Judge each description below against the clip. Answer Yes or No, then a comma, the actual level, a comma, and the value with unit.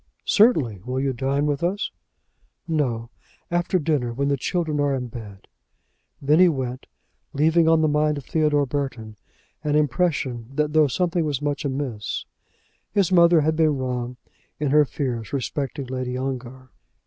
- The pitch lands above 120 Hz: Yes, medium, 140 Hz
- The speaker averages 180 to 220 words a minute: No, average, 155 wpm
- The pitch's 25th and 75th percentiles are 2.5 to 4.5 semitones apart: Yes, average, 3.5 semitones